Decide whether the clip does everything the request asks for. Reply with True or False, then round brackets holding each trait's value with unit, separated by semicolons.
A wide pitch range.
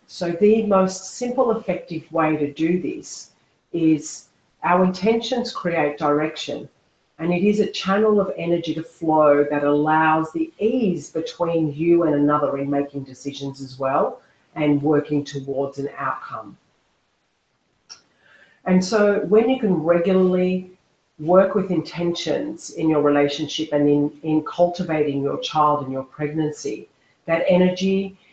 False (4.0 semitones)